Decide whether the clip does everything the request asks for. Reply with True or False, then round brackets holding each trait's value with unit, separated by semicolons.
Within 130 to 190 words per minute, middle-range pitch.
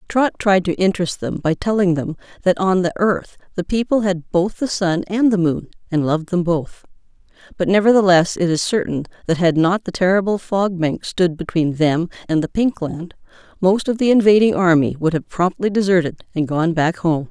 False (200 wpm; 180 Hz)